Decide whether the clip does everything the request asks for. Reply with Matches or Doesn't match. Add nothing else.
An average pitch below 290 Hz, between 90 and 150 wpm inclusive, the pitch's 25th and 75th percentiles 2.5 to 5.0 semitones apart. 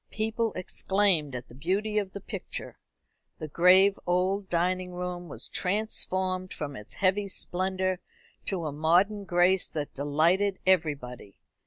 Matches